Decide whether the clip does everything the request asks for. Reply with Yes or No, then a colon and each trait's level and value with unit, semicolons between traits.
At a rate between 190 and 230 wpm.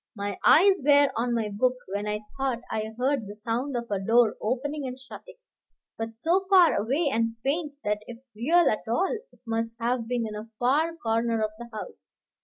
Yes: average, 200 wpm